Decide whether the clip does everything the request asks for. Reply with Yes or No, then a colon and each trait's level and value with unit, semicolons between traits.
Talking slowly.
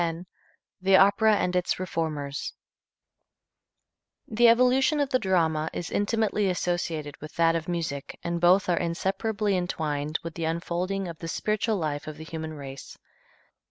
No: average, 150 wpm